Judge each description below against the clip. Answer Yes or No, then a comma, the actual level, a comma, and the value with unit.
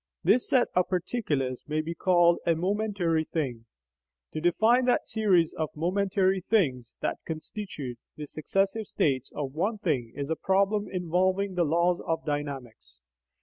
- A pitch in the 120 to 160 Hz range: No, medium, 170 Hz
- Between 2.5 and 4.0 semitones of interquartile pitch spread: No, average, 4.7 semitones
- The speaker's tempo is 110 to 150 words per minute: Yes, average, 145 wpm